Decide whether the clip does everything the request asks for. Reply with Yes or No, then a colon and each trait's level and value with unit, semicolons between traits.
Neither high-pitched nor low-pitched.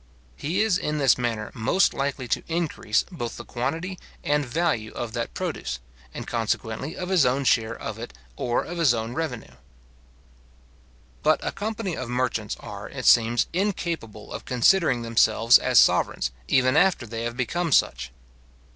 No: low, 125 Hz